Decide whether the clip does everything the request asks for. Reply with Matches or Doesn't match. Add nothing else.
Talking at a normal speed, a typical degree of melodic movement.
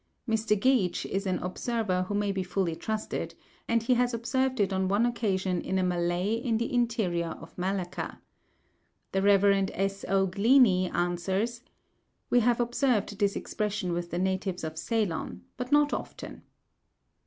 Matches